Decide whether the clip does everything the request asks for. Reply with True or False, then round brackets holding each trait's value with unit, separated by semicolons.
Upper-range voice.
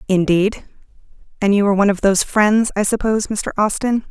True (205 Hz)